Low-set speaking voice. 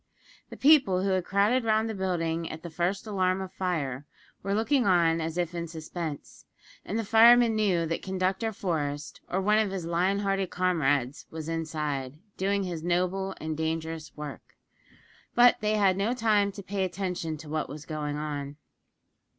No: medium, 180 Hz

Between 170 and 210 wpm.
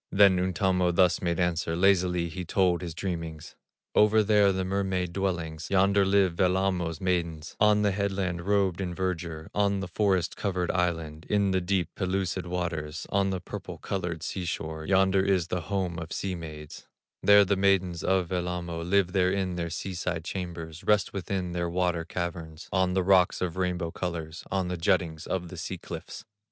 Yes: average, 175 wpm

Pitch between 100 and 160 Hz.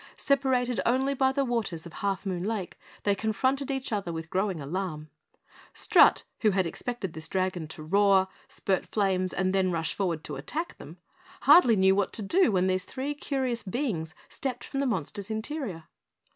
No: high, 200 Hz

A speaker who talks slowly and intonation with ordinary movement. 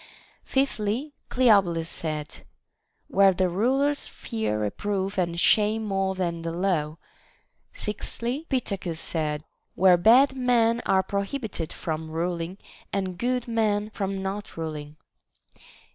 Yes: slow, 115 wpm; average, 4.9 semitones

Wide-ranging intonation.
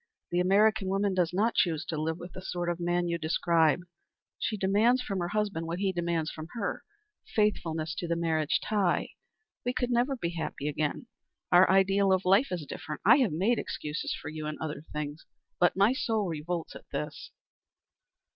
No: average, 3.8 semitones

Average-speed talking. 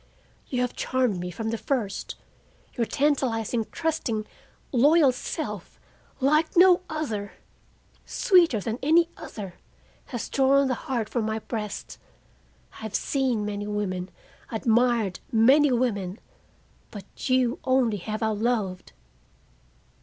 No: slow, 120 wpm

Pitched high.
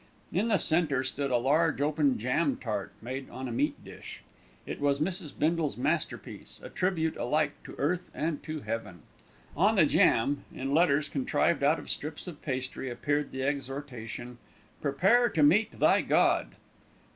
No: medium, 145 Hz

